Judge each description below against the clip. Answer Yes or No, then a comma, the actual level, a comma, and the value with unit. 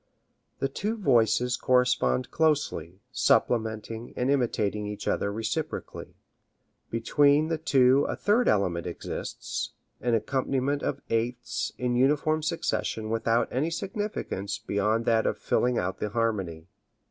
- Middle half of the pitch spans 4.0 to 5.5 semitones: Yes, average, 4.8 semitones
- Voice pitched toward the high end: No, low, 120 Hz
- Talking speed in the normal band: No, slow, 125 wpm